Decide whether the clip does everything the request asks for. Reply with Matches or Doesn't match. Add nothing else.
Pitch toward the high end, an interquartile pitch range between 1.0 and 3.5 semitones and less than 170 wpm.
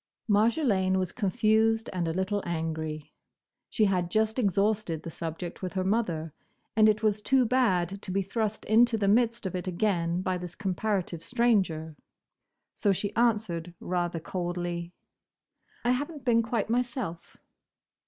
Doesn't match